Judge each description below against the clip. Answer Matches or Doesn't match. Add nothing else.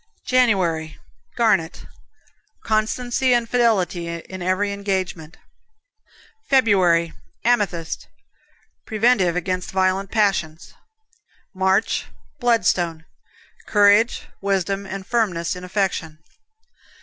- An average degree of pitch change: Matches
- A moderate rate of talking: Doesn't match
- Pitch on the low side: Doesn't match